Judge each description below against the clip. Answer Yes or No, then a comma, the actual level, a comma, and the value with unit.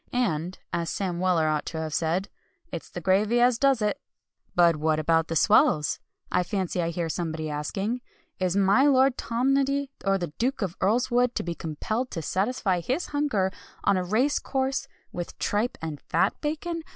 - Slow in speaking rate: No, average, 175 wpm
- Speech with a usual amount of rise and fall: No, wide, 6.9 semitones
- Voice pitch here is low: No, high, 195 Hz